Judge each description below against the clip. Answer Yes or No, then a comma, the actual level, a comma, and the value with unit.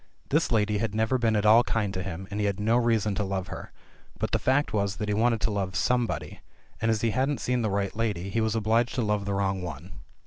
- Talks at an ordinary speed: No, fast, 255 wpm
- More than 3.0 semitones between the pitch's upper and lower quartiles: No, narrow, 2.5 semitones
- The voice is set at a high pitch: No, low, 105 Hz